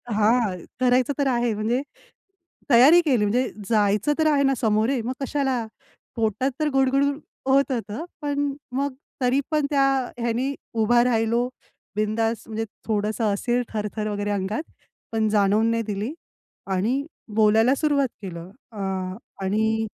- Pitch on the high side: Yes, high, 230 Hz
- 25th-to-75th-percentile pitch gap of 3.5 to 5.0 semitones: Yes, average, 3.9 semitones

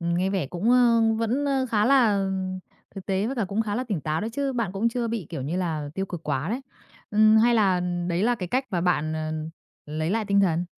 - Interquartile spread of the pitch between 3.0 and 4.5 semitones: No, average, 5.0 semitones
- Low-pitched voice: No, high, 200 Hz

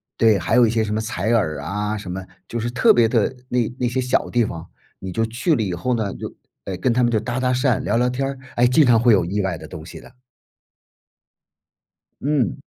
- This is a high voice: No, low, 115 Hz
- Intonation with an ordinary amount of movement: Yes, average, 3.4 semitones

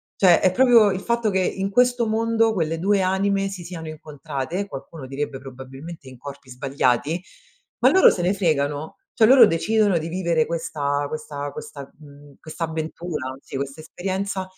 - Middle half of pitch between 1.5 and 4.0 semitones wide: No, wide, 5.4 semitones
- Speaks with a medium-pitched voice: Yes, medium, 165 Hz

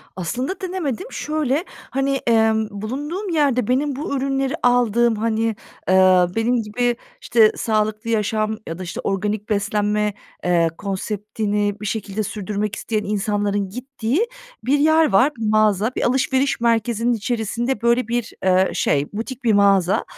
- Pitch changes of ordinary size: Yes, average, 3.6 semitones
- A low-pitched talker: No, high, 220 Hz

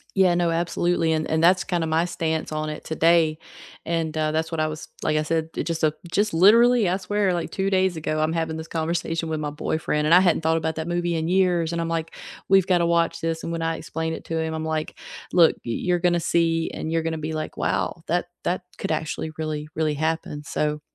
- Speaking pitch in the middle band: Yes, medium, 165 Hz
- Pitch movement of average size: No, narrow, 1.6 semitones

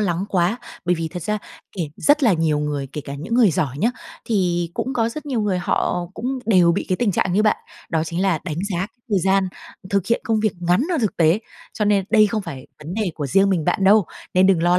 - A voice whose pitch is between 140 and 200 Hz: Yes, medium, 185 Hz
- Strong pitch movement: No, average, 4.1 semitones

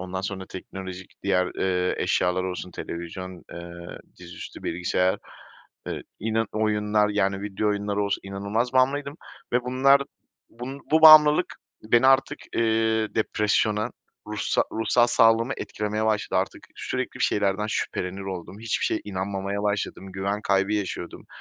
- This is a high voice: No, low, 105 Hz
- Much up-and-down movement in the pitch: No, average, 3.0 semitones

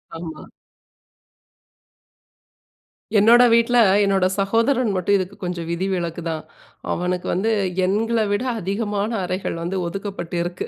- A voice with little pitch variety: No, average, 3.1 semitones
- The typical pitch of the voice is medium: No, high, 195 Hz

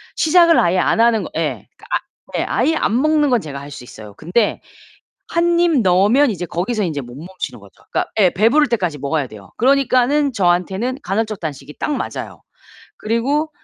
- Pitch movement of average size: No, wide, 8.3 semitones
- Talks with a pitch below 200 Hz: No, high, 215 Hz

